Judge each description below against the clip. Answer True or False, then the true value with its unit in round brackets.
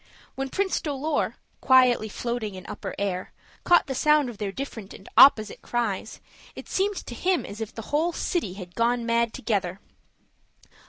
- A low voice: False (240 Hz)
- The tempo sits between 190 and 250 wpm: False (165 wpm)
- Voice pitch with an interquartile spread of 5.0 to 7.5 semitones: True (5.4 semitones)